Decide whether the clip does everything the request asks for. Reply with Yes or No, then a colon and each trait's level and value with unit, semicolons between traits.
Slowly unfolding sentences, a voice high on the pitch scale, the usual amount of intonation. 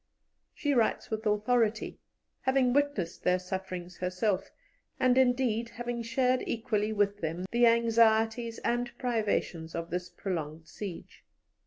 Yes: slow, 125 wpm; high, 220 Hz; average, 4.8 semitones